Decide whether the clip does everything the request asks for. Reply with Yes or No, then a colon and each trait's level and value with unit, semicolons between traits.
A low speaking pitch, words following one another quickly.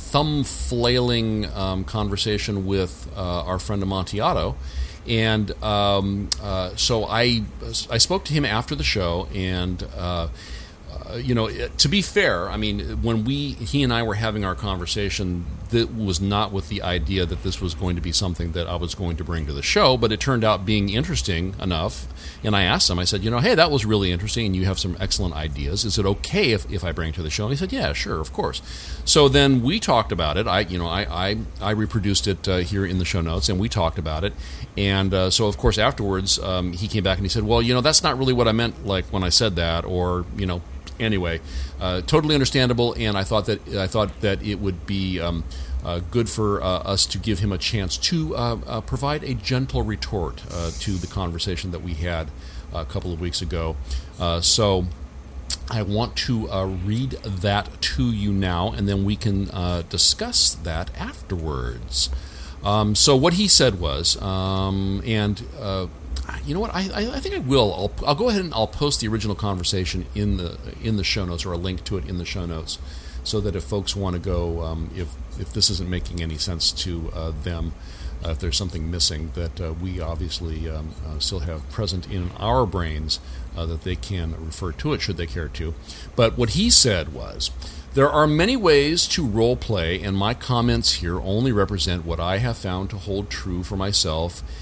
Yes: very low, 95 Hz; fast, 215 wpm